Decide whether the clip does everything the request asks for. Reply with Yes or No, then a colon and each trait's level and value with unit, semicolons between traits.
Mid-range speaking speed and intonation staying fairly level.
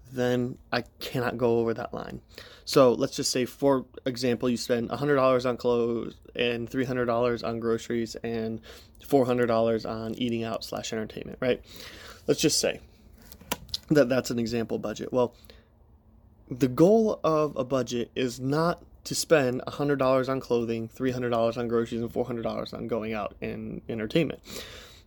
Yes: average, 145 wpm; narrow, 2.1 semitones